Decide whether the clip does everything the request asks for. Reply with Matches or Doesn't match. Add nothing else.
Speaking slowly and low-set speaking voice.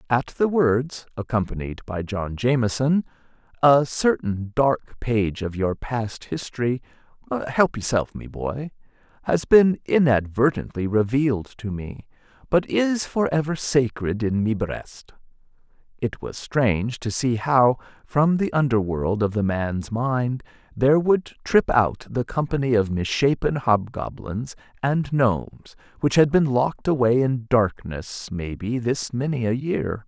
Matches